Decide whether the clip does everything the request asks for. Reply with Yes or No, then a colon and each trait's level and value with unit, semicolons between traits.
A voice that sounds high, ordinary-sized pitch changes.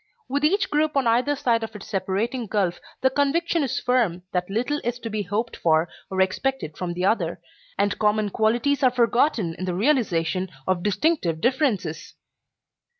No: high, 225 Hz; wide, 6.0 semitones